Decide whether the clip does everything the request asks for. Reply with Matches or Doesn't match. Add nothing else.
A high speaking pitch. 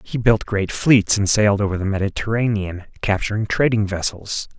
Doesn't match